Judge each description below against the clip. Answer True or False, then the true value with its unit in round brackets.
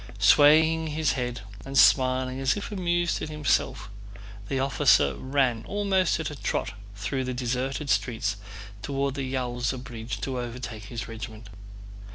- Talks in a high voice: False (130 Hz)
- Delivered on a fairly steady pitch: False (3.4 semitones)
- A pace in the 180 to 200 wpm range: False (145 wpm)